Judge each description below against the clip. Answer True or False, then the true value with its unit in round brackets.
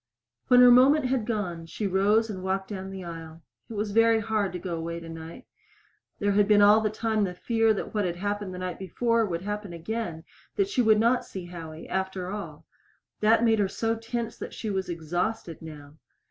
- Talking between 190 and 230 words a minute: True (200 wpm)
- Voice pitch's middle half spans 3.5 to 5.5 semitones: True (4.1 semitones)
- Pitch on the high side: True (205 Hz)